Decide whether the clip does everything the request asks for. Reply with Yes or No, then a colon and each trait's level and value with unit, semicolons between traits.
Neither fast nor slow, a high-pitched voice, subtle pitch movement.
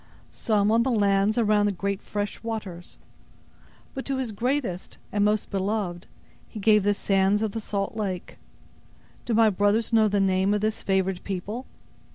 Yes: average, 170 wpm; high, 205 Hz; narrow, 2.1 semitones